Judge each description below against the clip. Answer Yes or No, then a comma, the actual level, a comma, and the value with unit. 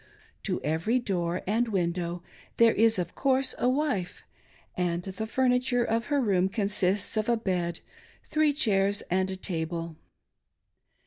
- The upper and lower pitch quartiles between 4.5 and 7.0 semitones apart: Yes, average, 5.0 semitones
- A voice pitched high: Yes, high, 200 Hz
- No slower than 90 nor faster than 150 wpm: Yes, average, 140 wpm